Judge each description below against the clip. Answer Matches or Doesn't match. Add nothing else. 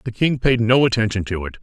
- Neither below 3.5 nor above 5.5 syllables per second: Doesn't match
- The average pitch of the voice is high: Doesn't match